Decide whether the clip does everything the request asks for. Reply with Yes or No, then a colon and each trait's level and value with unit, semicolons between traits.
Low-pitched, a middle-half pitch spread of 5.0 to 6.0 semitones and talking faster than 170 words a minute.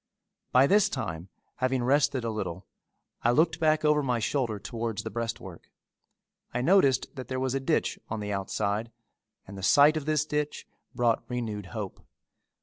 No: low, 125 Hz; average, 5.3 semitones; average, 165 wpm